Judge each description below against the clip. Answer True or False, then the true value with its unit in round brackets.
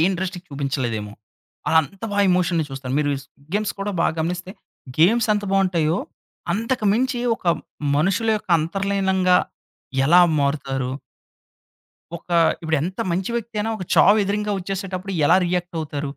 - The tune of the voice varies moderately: True (4.4 semitones)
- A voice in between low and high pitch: True (180 Hz)